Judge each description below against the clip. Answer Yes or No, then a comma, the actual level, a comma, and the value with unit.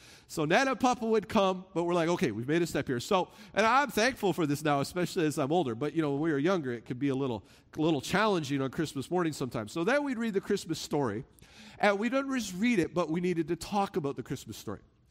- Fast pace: Yes, fast, 260 wpm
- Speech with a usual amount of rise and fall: No, wide, 6.0 semitones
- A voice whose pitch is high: No, medium, 170 Hz